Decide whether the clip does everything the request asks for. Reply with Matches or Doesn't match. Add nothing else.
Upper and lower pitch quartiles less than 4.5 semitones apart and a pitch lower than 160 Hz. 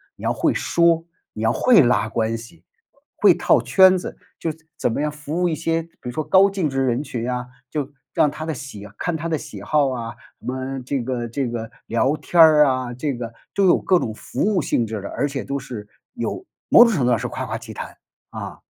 Doesn't match